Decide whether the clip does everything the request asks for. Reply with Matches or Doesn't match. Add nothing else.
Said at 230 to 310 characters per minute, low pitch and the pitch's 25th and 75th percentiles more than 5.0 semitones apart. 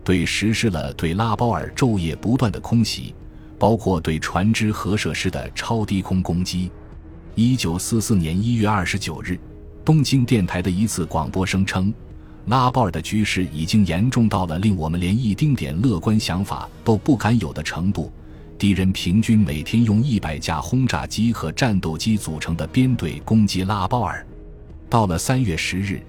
Matches